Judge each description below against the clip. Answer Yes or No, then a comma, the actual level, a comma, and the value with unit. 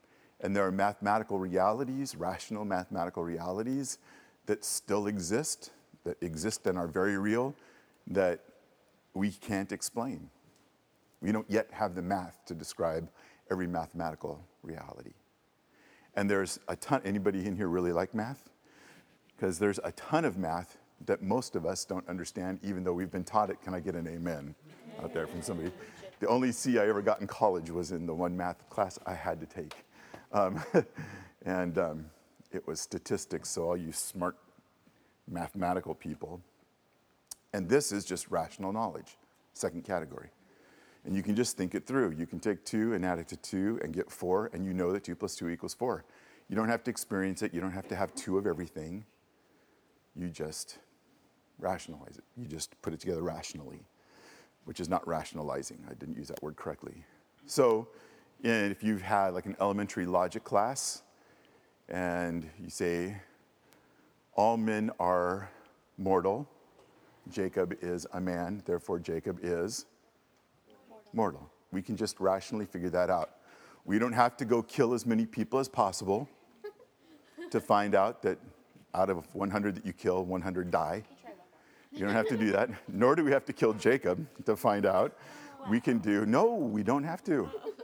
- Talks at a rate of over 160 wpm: Yes, average, 170 wpm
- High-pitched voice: No, very low, 95 Hz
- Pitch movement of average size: Yes, average, 3.4 semitones